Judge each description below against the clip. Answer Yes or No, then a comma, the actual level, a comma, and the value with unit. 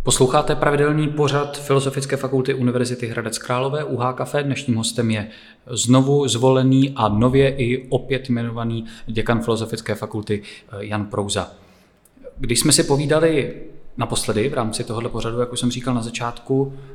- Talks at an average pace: Yes, average, 140 wpm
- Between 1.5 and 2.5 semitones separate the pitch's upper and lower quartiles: No, average, 2.9 semitones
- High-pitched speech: No, low, 125 Hz